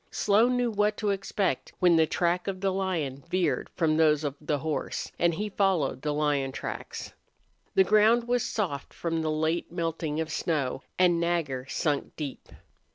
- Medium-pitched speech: Yes, medium, 170 Hz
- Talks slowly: No, average, 170 wpm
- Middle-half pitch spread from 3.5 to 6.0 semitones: Yes, average, 4.3 semitones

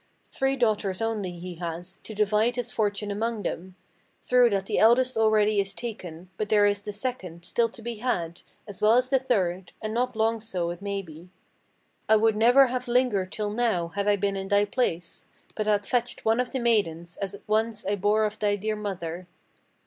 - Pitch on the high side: Yes, high, 210 Hz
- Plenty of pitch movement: No, average, 3.1 semitones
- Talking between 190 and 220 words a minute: Yes, average, 200 wpm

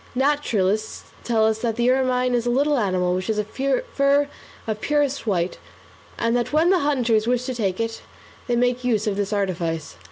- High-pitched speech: Yes, high, 235 Hz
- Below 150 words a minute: No, average, 190 wpm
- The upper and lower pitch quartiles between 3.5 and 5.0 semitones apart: Yes, average, 4.0 semitones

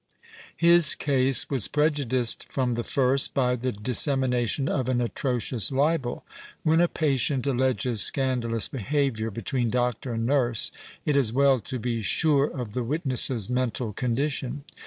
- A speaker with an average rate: Yes, average, 145 wpm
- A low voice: Yes, low, 130 Hz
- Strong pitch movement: No, average, 2.7 semitones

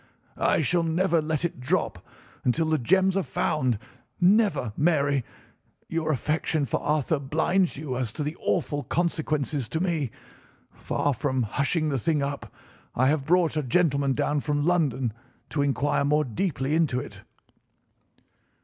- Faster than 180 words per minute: No, average, 145 wpm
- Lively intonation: No, average, 3.2 semitones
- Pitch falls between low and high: Yes, medium, 150 Hz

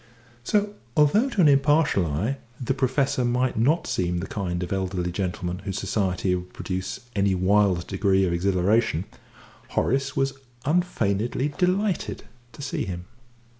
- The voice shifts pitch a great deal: Yes, wide, 7.1 semitones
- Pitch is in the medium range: No, low, 100 Hz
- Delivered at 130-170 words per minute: Yes, average, 140 wpm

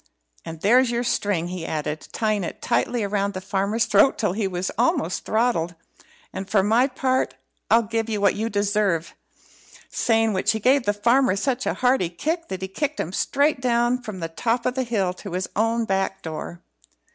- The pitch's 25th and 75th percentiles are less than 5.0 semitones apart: Yes, average, 4.2 semitones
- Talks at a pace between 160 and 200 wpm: Yes, average, 190 wpm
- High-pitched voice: Yes, high, 210 Hz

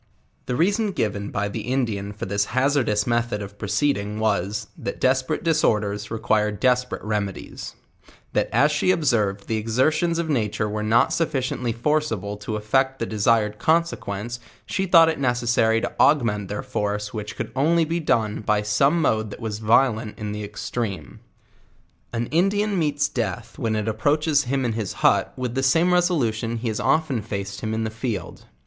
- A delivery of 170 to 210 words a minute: Yes, average, 180 wpm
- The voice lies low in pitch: Yes, low, 115 Hz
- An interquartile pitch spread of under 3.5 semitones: No, average, 5.1 semitones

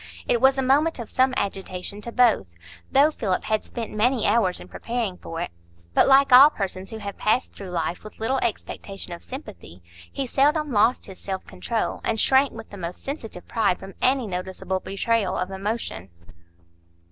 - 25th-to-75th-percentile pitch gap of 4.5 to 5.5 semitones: Yes, average, 5.2 semitones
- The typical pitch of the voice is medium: No, high, 220 Hz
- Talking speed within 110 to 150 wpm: No, average, 180 wpm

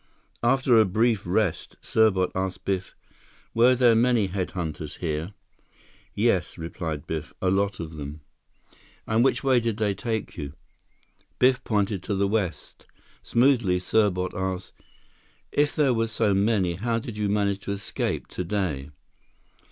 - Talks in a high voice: No, low, 100 Hz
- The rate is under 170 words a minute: Yes, average, 145 wpm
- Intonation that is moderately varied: Yes, average, 3.9 semitones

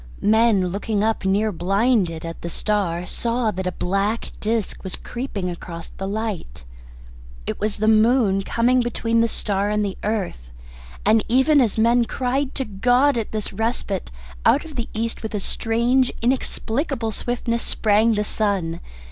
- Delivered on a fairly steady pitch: No, average, 3.2 semitones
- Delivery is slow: No, average, 160 wpm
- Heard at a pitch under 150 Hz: No, high, 220 Hz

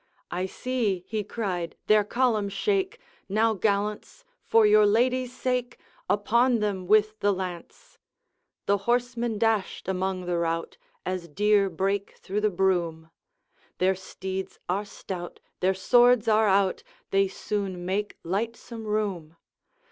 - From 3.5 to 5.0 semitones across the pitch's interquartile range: No, average, 3.0 semitones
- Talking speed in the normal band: No, slow, 130 wpm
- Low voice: No, high, 205 Hz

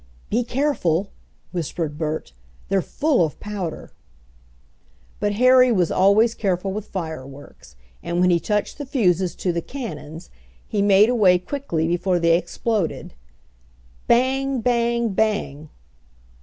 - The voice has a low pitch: No, high, 195 Hz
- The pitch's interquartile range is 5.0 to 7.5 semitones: Yes, wide, 5.6 semitones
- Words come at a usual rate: No, slow, 125 wpm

